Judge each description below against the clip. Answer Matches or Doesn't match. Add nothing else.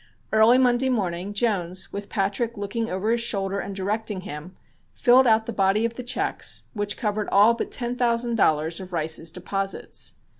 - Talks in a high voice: Matches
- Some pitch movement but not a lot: Matches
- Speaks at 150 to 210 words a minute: Matches